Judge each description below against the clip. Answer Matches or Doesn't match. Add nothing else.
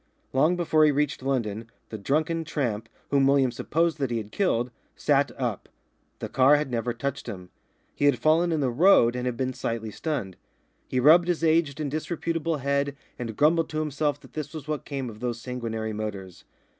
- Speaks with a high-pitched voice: Doesn't match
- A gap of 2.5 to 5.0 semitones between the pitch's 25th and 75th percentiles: Matches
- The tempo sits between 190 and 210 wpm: Matches